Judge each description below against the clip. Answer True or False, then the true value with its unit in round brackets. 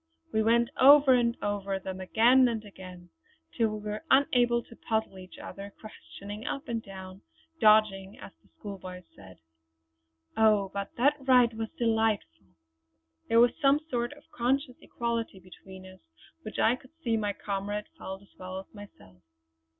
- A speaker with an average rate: True (160 wpm)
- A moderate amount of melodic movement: True (3.7 semitones)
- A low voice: False (215 Hz)